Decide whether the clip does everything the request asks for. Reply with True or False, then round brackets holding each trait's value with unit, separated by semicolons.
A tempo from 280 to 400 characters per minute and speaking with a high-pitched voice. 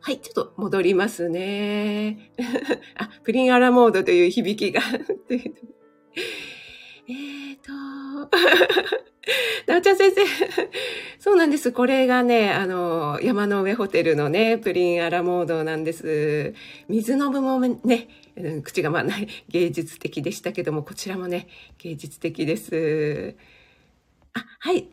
False (250 characters per minute; 225 Hz)